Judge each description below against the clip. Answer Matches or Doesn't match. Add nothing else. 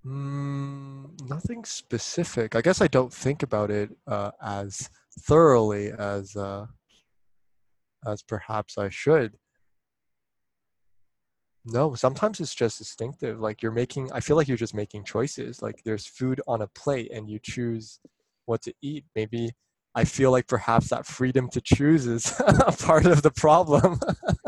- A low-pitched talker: Matches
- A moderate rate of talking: Matches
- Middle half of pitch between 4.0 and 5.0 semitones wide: Matches